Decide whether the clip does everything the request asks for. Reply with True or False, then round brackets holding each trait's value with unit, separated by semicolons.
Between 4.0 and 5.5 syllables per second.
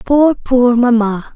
False (3.4 syllables/s)